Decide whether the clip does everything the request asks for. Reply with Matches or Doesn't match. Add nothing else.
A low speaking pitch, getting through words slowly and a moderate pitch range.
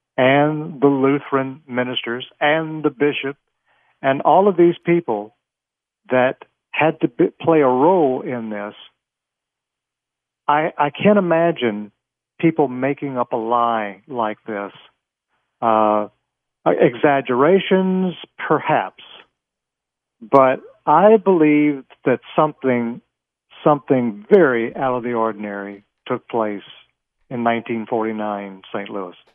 Matches